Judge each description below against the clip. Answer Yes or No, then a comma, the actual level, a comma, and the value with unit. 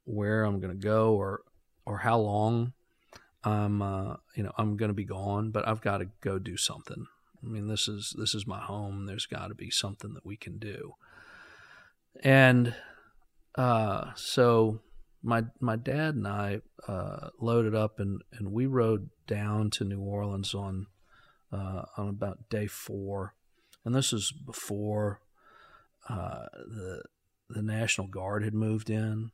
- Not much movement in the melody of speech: Yes, narrow, 2.1 semitones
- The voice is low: Yes, low, 105 Hz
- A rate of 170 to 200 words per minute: No, average, 155 wpm